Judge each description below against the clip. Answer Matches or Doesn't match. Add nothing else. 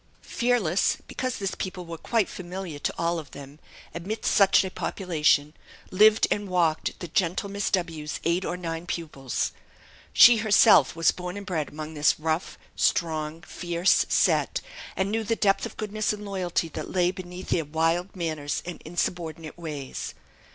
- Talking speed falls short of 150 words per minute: Doesn't match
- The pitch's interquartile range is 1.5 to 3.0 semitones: Doesn't match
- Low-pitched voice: Doesn't match